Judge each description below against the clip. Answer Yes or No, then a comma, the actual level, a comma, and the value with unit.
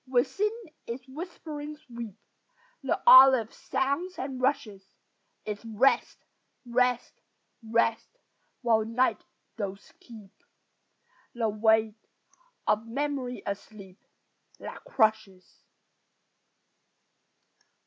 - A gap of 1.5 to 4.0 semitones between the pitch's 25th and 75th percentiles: Yes, average, 3.6 semitones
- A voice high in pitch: Yes, high, 235 Hz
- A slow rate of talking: Yes, slow, 80 wpm